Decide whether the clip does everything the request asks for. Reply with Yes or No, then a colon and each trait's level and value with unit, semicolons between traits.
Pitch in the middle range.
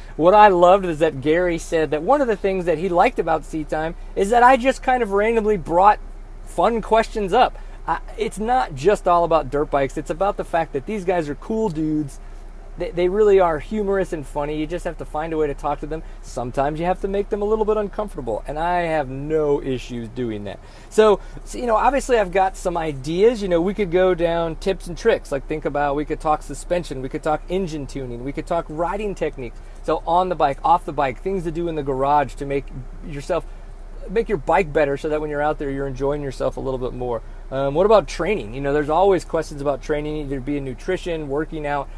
Yes: medium, 160 Hz